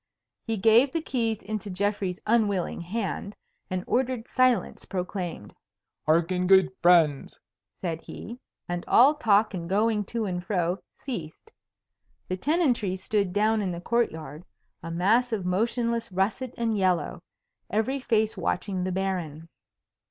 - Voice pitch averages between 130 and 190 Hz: No, high, 200 Hz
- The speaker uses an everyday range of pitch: Yes, average, 4.2 semitones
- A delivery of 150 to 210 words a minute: No, slow, 135 wpm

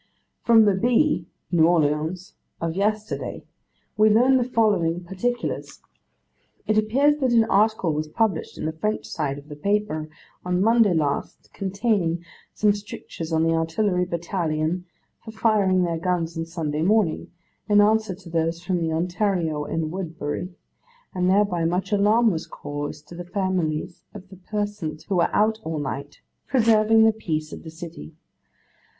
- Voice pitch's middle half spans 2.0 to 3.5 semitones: No, average, 4.7 semitones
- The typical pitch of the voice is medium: Yes, medium, 180 Hz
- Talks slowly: No, average, 155 wpm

